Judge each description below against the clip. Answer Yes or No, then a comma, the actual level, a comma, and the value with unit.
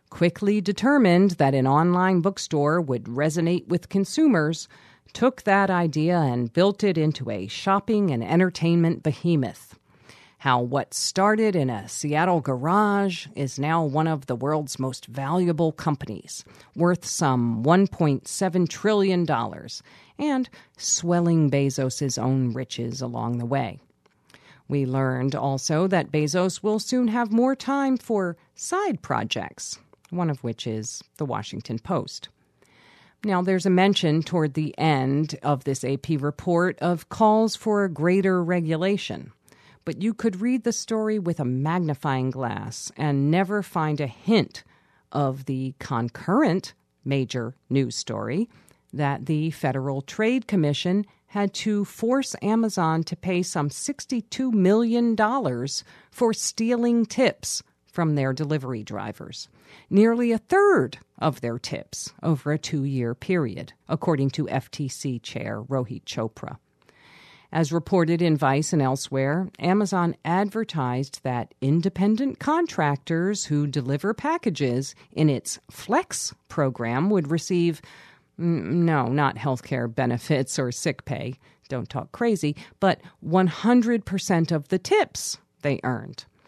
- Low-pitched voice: No, medium, 160 Hz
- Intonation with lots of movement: Yes, wide, 6.3 semitones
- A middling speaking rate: No, slow, 125 wpm